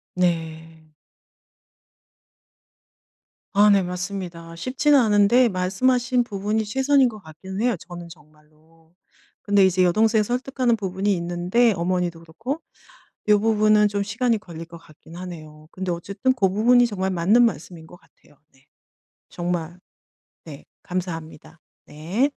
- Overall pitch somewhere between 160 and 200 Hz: Yes, medium, 185 Hz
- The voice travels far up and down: No, average, 4.7 semitones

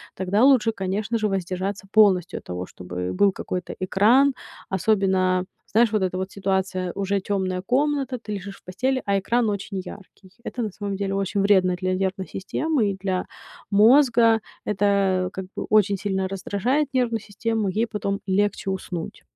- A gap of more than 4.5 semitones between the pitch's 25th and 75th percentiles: No, average, 2.7 semitones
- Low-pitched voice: No, high, 200 Hz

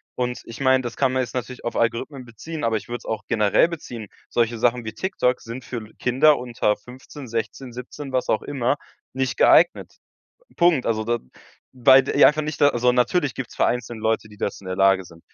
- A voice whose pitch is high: No, low, 125 Hz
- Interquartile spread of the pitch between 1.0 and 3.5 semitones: Yes, narrow, 2.6 semitones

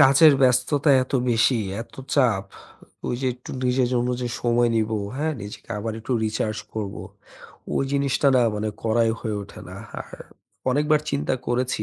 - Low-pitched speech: Yes, low, 125 Hz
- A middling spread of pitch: Yes, average, 3.6 semitones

